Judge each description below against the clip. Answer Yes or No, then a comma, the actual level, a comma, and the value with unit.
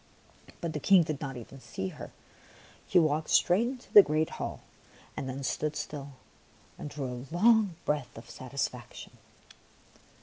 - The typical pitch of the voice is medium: Yes, medium, 150 Hz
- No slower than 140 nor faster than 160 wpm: Yes, average, 155 wpm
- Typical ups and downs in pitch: Yes, average, 4.5 semitones